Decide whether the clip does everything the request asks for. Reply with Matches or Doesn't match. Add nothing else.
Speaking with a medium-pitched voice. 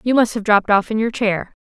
Doesn't match